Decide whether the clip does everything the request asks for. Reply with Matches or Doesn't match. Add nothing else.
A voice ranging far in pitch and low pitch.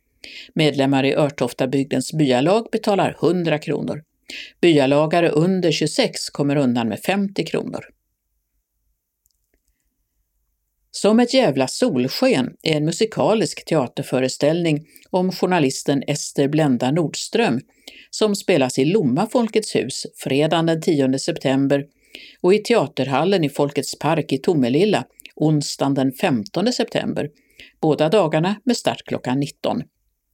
Doesn't match